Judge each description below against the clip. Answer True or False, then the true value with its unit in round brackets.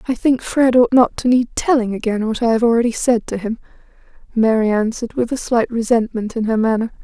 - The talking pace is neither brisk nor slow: False (215 wpm)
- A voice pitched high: True (230 Hz)